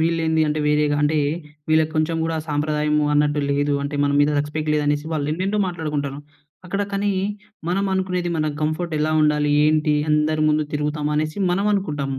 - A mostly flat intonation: Yes, narrow, 1.6 semitones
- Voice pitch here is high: No, medium, 155 Hz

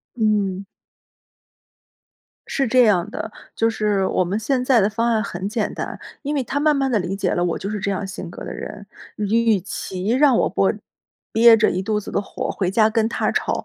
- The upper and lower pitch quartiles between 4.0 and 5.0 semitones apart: No, average, 3.1 semitones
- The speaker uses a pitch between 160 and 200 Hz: No, high, 215 Hz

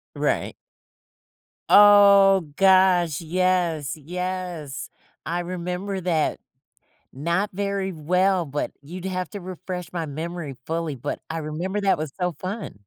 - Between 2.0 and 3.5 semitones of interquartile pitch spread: Yes, average, 2.9 semitones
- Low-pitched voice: No, medium, 180 Hz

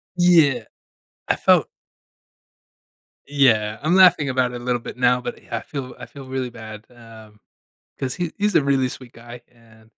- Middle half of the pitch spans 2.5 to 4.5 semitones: Yes, average, 3.2 semitones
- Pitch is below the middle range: Yes, low, 125 Hz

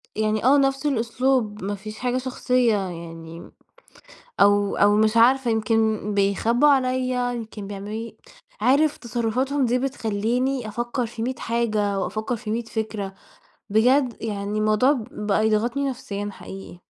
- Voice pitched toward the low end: No, high, 225 Hz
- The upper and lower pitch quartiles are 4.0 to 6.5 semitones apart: No, average, 3.3 semitones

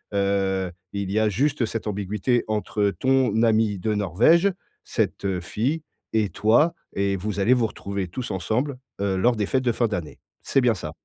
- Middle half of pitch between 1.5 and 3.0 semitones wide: No, average, 3.6 semitones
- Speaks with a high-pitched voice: No, low, 105 Hz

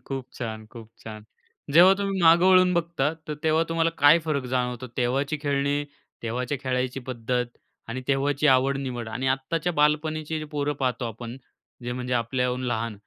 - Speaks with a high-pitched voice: No, low, 135 Hz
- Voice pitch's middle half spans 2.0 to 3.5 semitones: No, average, 3.9 semitones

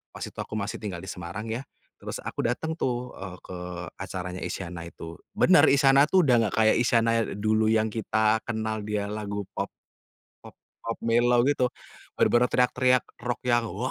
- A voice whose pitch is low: Yes, low, 110 Hz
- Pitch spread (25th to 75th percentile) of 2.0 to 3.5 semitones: Yes, average, 3.2 semitones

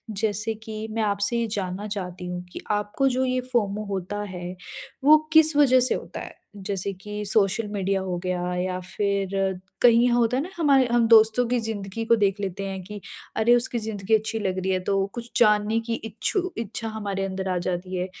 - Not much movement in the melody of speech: No, average, 3.2 semitones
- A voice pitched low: No, high, 210 Hz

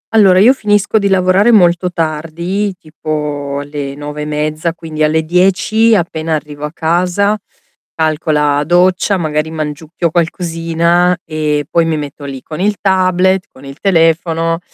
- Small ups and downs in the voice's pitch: No, average, 3.3 semitones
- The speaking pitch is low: No, medium, 165 Hz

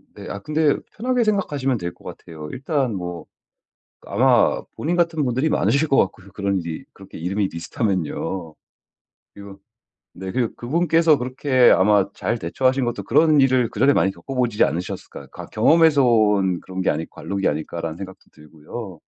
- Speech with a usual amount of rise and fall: No, wide, 6.9 semitones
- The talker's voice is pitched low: Yes, low, 110 Hz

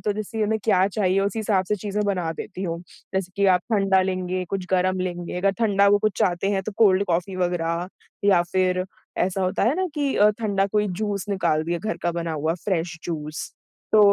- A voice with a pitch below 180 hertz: No, high, 190 Hz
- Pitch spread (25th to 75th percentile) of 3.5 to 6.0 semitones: No, narrow, 2.5 semitones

